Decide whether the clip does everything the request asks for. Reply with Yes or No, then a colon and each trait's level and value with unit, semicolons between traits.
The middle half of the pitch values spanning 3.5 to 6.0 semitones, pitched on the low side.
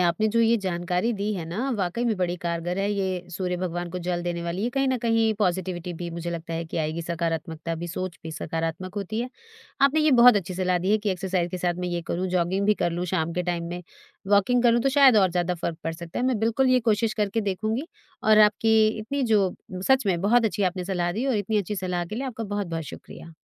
No: average, 4.0 semitones; medium, 185 Hz